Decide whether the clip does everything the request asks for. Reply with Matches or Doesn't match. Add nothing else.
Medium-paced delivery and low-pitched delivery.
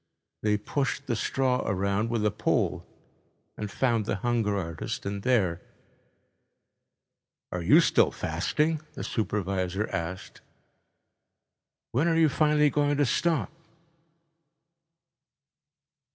Doesn't match